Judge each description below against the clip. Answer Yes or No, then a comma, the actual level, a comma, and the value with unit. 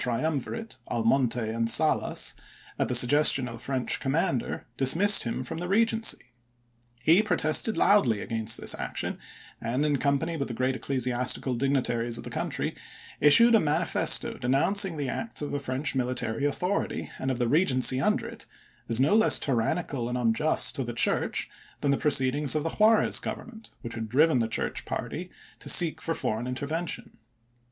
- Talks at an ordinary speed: Yes, average, 170 wpm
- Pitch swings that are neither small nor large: Yes, average, 4.8 semitones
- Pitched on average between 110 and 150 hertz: Yes, low, 135 Hz